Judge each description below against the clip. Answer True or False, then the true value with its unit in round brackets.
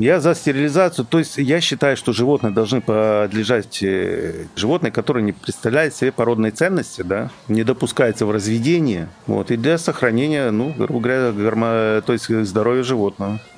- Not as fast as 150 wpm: False (155 wpm)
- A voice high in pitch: False (120 Hz)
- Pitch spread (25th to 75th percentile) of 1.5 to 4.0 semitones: False (4.7 semitones)